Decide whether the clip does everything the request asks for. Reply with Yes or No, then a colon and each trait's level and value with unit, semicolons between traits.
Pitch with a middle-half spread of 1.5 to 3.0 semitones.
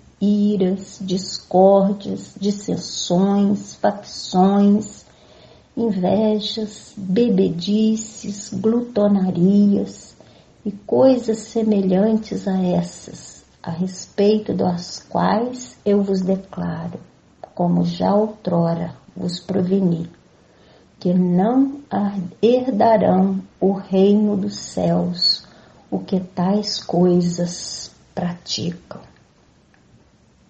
Yes: average, 2.7 semitones